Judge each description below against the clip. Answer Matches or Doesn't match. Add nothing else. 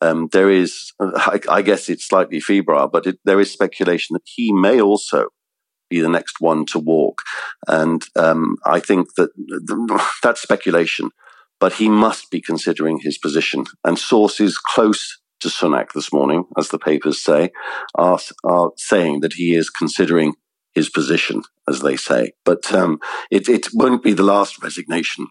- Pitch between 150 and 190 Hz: Doesn't match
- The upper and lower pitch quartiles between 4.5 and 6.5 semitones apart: Doesn't match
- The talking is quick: Doesn't match